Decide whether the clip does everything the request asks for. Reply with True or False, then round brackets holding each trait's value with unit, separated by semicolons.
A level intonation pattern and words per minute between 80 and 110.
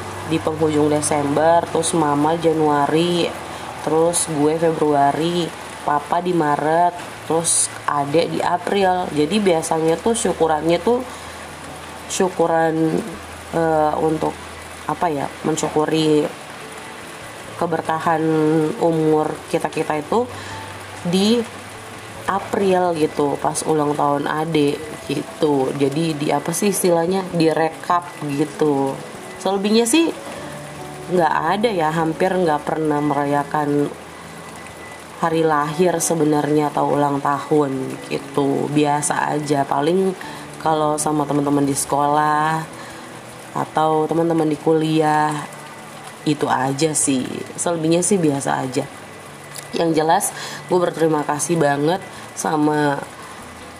True (2.3 semitones; 100 wpm)